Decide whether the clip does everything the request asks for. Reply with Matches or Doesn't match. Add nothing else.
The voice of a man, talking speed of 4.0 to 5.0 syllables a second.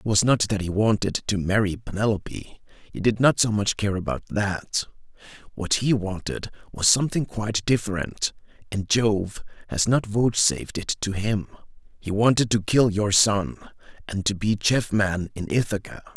Matches